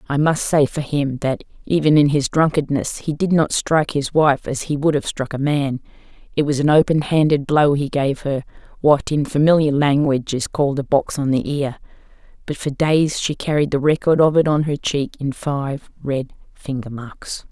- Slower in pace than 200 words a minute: No, fast, 205 wpm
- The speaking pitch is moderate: Yes, medium, 145 Hz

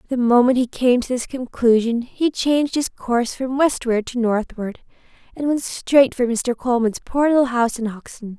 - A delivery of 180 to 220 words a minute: Yes, average, 185 wpm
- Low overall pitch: No, high, 245 Hz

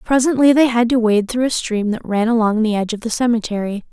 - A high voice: Yes, high, 230 Hz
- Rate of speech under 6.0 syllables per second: No, 6.1 syllables/s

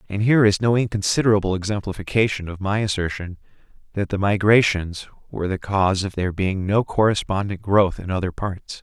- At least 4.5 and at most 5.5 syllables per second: No, 5.9 syllables/s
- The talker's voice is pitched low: Yes, low, 100 Hz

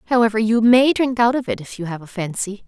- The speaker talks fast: Yes, fast, 270 wpm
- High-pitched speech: Yes, high, 220 Hz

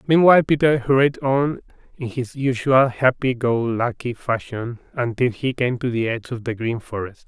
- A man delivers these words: Yes, male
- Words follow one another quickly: No, average, 175 wpm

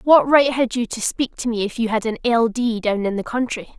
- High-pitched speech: Yes, high, 230 Hz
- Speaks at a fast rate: Yes, fast, 285 wpm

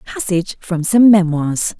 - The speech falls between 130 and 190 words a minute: Yes, slow, 135 wpm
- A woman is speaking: Yes, female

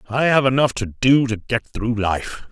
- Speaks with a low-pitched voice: Yes, low, 120 Hz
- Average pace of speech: No, fast, 215 wpm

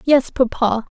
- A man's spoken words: No, female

